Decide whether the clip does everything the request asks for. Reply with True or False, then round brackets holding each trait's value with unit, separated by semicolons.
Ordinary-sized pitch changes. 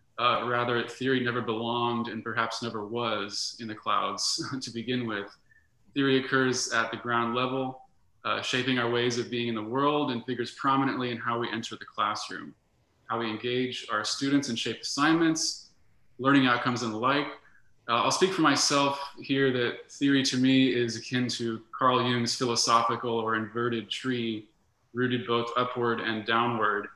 False (2.0 semitones)